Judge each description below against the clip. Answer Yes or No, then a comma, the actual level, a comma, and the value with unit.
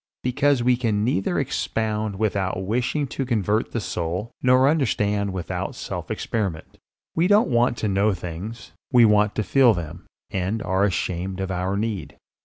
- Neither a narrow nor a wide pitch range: Yes, average, 4.2 semitones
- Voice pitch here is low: Yes, low, 105 Hz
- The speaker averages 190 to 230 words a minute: No, average, 160 wpm